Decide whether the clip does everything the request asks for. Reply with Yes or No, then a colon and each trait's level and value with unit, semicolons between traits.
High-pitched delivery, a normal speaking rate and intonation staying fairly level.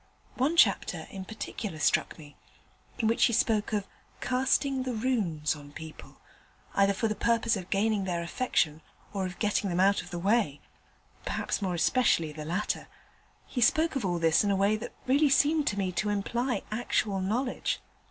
No: high, 205 Hz; average, 180 wpm; average, 5.2 semitones